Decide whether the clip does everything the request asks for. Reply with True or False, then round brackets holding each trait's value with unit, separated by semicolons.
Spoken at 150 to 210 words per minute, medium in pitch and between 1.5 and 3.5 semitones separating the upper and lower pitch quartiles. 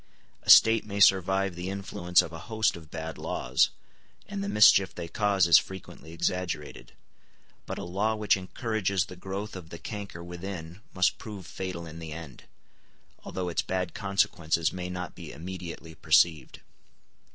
False (160 wpm; 90 Hz; 2.8 semitones)